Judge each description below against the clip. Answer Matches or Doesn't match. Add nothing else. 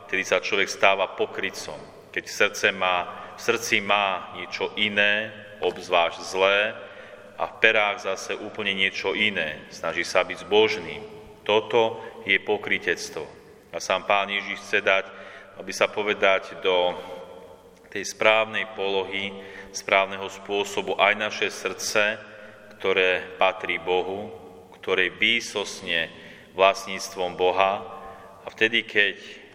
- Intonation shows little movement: Matches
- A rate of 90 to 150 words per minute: Matches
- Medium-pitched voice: Doesn't match